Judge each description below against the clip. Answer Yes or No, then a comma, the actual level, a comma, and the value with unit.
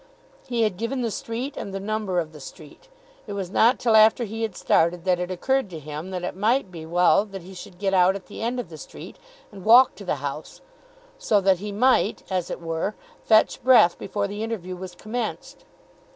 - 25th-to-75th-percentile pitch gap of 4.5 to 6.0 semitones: No, average, 4.0 semitones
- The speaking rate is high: Yes, fast, 225 wpm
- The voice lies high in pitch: Yes, high, 195 Hz